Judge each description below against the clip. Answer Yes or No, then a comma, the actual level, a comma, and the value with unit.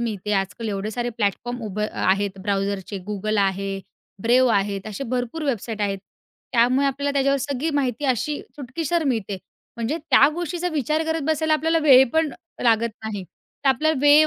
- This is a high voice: Yes, high, 245 Hz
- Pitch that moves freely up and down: Yes, wide, 5.9 semitones